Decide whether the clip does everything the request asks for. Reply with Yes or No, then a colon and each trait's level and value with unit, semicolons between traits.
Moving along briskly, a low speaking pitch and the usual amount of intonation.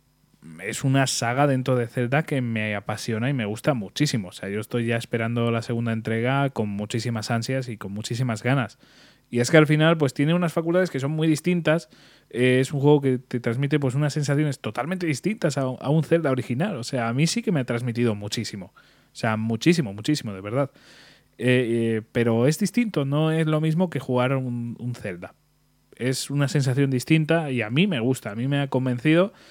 Yes: fast, 210 wpm; low, 130 Hz; average, 4.4 semitones